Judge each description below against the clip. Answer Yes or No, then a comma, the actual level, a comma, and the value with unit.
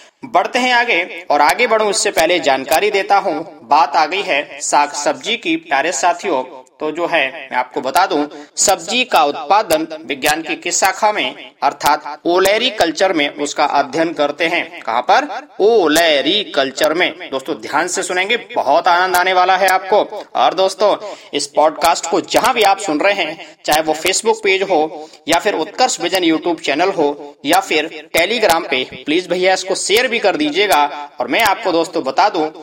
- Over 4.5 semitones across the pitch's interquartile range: Yes, average, 5.1 semitones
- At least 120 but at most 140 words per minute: No, average, 180 wpm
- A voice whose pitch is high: No, medium, 180 Hz